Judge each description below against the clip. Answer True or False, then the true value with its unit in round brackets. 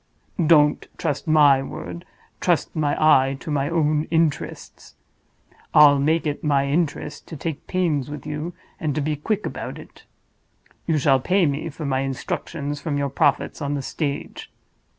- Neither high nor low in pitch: True (150 Hz)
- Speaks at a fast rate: False (160 wpm)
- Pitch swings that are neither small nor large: False (2.0 semitones)